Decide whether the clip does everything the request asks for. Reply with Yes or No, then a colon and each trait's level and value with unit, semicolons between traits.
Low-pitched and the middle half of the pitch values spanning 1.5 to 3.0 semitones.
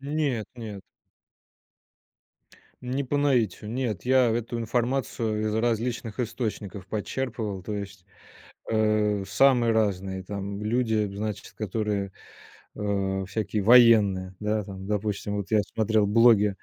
Yes: low, 110 Hz; average, 2.7 semitones